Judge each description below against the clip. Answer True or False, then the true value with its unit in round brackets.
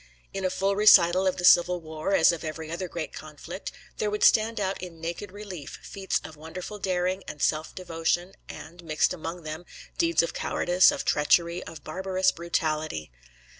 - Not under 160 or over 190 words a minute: True (175 wpm)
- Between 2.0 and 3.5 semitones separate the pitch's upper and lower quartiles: True (2.8 semitones)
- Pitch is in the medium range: True (175 Hz)